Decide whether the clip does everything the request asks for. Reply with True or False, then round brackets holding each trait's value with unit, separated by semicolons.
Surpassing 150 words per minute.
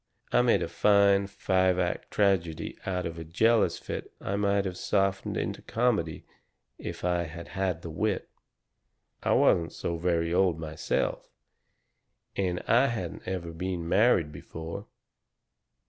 False (140 wpm)